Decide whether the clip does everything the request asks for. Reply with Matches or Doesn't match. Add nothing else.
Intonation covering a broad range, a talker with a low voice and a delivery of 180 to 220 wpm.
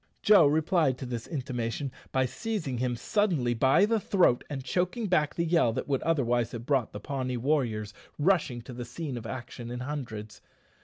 Doesn't match